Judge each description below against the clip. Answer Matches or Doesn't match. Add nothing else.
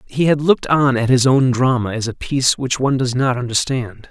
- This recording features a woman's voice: Doesn't match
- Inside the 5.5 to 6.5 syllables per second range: Matches